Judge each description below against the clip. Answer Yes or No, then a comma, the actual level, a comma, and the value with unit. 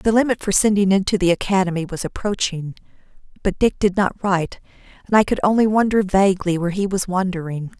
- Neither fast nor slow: Yes, average, 190 wpm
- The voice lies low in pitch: No, high, 190 Hz